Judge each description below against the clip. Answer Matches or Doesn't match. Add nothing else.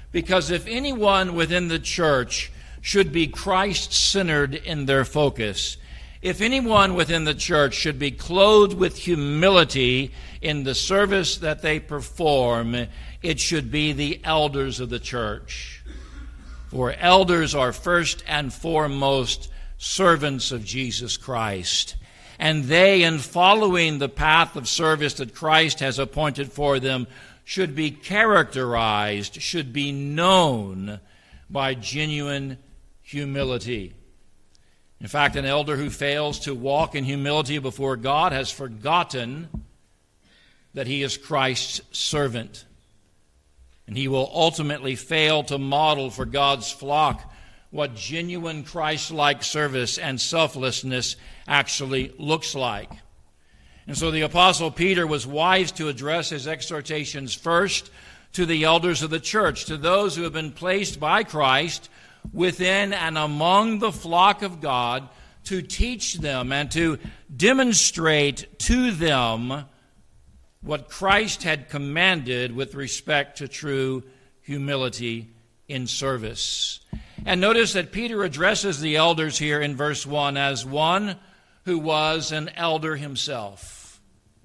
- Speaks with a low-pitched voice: Doesn't match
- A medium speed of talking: Doesn't match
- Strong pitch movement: Doesn't match